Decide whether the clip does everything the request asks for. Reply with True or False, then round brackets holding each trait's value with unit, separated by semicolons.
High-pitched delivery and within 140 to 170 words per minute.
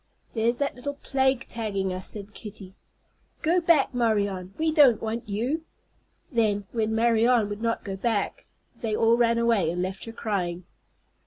True (225 Hz; 160 wpm)